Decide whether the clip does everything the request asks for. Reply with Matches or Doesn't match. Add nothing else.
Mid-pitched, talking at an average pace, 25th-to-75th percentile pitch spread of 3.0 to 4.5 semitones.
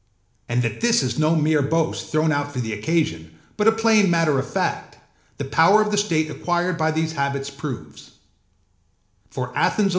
Matches